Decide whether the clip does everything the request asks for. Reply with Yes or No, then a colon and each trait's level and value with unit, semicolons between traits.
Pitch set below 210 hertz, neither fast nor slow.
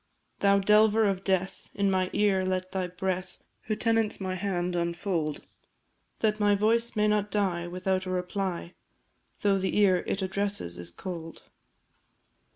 Yes: high, 190 Hz; average, 150 wpm